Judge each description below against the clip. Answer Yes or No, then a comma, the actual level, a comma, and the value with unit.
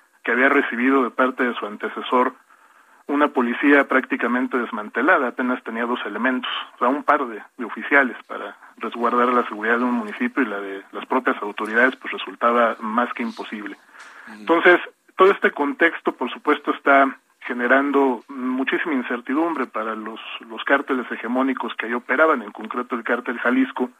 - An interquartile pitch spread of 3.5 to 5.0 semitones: No, narrow, 2.6 semitones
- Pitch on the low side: Yes, low, 130 Hz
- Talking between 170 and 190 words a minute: No, average, 160 wpm